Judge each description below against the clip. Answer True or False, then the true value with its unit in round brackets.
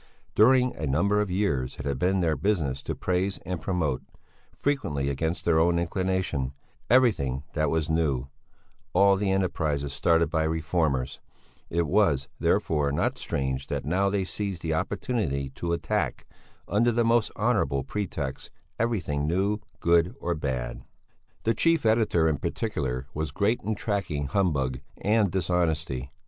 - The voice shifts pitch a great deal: True (5.8 semitones)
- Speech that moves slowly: False (145 wpm)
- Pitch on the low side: True (85 Hz)